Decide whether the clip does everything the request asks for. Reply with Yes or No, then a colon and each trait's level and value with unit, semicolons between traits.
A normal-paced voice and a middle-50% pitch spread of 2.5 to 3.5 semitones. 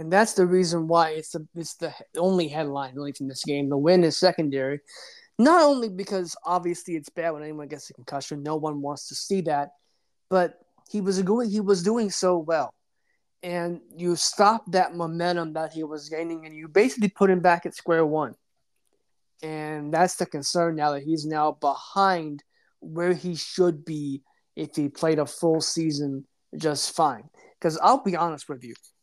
Yes: average, 185 wpm; average, 3.2 semitones